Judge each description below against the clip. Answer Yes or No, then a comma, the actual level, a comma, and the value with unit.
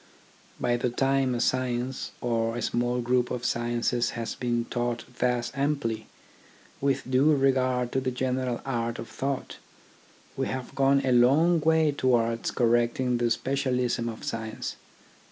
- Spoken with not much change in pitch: Yes, narrow, 1.9 semitones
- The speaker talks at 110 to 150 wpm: Yes, average, 145 wpm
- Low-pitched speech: Yes, low, 125 Hz